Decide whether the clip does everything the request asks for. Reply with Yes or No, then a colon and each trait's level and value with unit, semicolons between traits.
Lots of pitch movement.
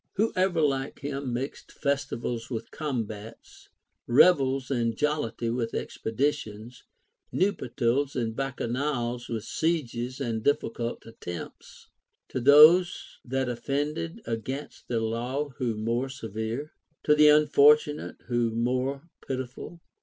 No: average, 3.9 semitones